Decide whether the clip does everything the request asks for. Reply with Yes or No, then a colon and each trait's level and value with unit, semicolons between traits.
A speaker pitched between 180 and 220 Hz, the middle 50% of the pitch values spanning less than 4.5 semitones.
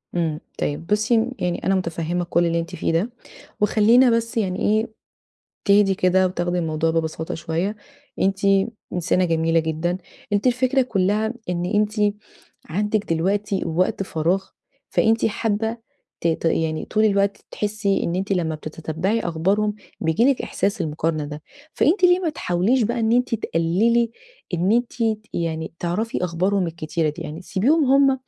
No: high, 190 Hz; average, 4.9 semitones